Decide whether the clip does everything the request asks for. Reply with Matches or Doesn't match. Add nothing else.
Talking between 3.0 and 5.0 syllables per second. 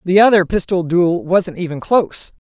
Matches